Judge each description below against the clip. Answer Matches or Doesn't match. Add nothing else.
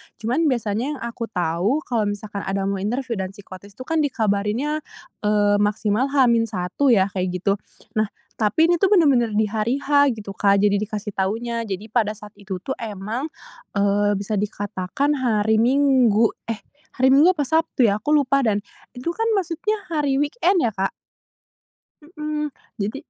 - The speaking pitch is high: Matches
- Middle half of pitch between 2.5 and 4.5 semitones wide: Doesn't match